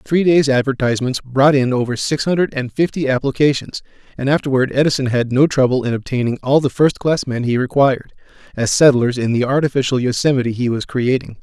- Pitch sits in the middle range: No, low, 130 Hz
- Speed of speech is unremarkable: Yes, average, 180 wpm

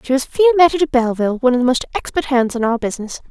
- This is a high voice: Yes, very high, 265 Hz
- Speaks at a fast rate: Yes, fast, 255 wpm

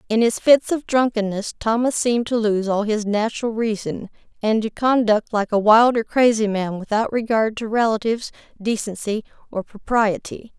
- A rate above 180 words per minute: No, average, 165 wpm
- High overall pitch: Yes, high, 220 Hz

